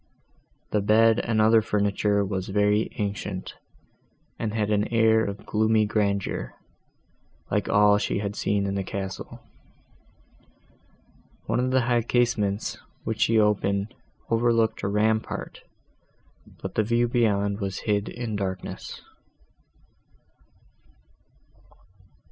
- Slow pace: Yes, slow, 115 wpm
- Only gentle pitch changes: Yes, narrow, 2.0 semitones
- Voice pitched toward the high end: No, low, 105 Hz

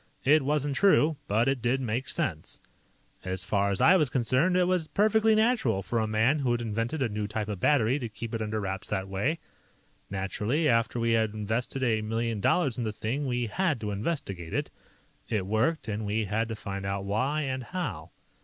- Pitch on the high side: No, low, 115 Hz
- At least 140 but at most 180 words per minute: No, fast, 205 wpm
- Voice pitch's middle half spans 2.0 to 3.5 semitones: No, average, 5.3 semitones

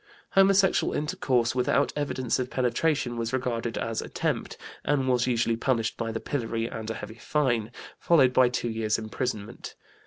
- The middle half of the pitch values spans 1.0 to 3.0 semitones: Yes, narrow, 2.5 semitones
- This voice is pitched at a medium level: No, low, 120 Hz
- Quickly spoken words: No, average, 155 wpm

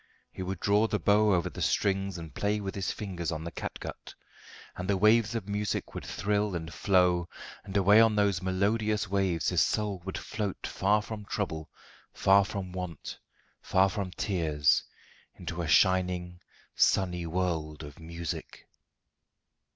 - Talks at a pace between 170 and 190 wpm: No, average, 155 wpm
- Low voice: Yes, very low, 95 Hz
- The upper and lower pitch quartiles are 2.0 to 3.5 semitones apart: Yes, average, 2.8 semitones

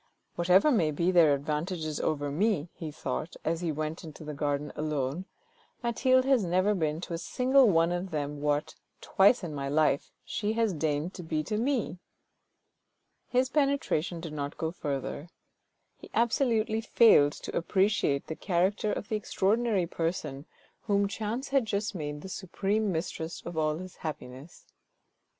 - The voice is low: No, medium, 170 Hz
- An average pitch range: No, wide, 5.7 semitones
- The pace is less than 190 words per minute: Yes, average, 165 wpm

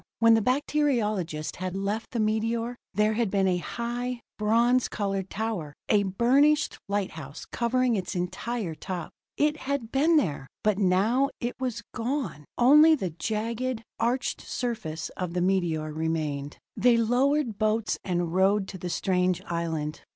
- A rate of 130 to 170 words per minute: Yes, average, 145 wpm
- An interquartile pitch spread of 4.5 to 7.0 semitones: Yes, average, 5.1 semitones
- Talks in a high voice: Yes, high, 215 Hz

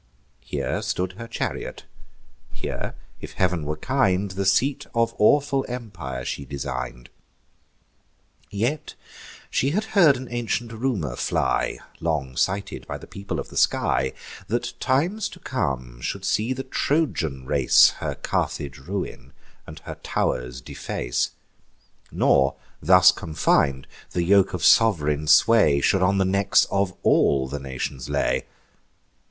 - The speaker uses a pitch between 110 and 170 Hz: No, very low, 95 Hz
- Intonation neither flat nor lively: No, wide, 8.9 semitones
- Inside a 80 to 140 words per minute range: Yes, slow, 135 wpm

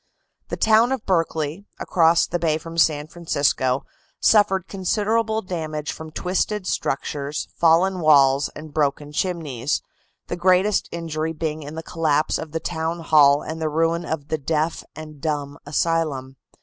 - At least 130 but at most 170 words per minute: Yes, average, 150 wpm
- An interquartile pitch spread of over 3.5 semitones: No, average, 2.7 semitones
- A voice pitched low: No, medium, 160 Hz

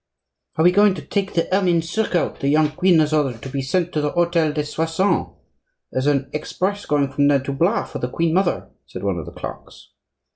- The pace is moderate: No, fast, 220 wpm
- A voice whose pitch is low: No, medium, 155 Hz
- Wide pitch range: No, average, 4.0 semitones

